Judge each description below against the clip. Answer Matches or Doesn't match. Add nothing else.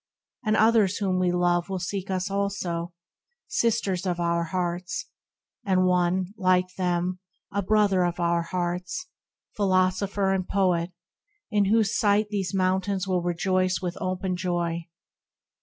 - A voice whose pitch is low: Doesn't match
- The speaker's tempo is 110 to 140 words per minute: Matches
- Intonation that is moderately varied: Doesn't match